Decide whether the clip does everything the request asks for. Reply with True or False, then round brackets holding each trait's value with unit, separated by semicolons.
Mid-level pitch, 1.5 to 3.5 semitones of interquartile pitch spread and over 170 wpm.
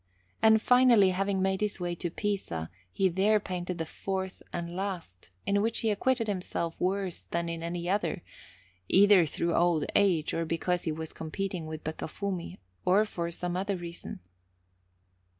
False (180 Hz; 2.9 semitones; 160 wpm)